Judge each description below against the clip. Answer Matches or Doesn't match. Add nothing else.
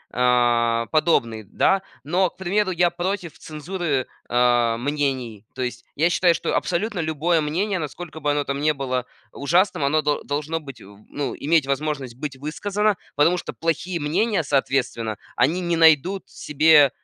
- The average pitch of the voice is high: Doesn't match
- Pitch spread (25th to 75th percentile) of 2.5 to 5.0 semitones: Matches